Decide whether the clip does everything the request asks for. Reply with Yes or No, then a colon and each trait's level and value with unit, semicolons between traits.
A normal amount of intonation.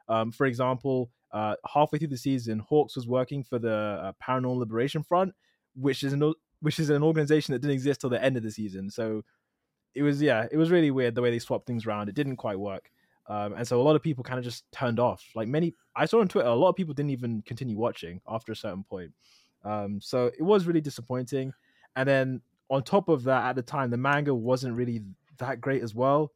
Yes: average, 3.8 semitones